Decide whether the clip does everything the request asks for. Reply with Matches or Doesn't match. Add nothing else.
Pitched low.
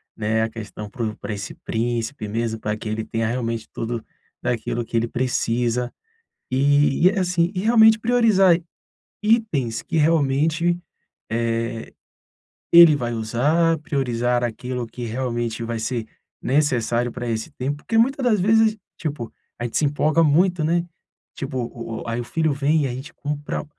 Matches